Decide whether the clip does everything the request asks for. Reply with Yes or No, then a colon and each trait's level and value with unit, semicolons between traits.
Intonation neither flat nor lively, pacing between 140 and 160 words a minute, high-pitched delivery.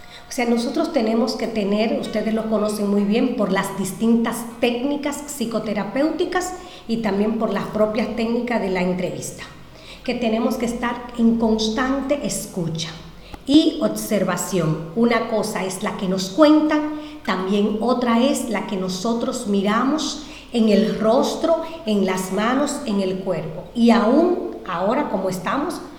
Yes: average, 4.7 semitones; average, 145 wpm; high, 225 Hz